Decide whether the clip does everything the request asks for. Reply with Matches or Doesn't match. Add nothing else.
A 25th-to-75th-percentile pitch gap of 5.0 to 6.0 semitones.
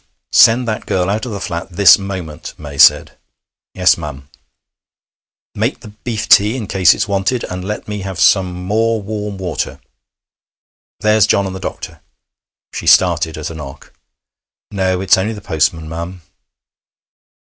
Doesn't match